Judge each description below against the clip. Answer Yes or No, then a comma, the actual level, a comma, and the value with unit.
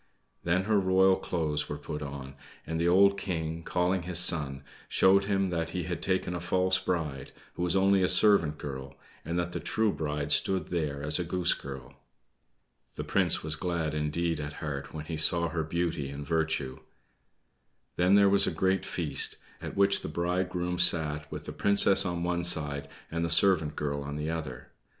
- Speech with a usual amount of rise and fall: Yes, average, 3.4 semitones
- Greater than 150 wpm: Yes, average, 185 wpm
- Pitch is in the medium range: No, very low, 85 Hz